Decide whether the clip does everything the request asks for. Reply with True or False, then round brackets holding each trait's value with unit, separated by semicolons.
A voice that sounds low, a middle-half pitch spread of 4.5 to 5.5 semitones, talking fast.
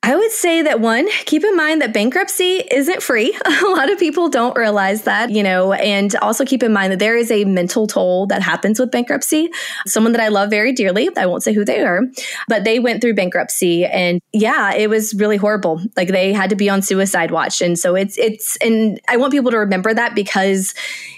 False (220 Hz; 5.0 semitones; 225 wpm)